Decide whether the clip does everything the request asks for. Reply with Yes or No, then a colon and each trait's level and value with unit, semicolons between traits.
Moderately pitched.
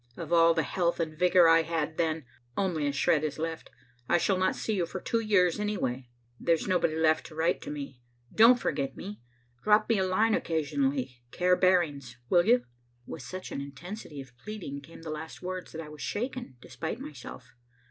Yes: medium, 165 Hz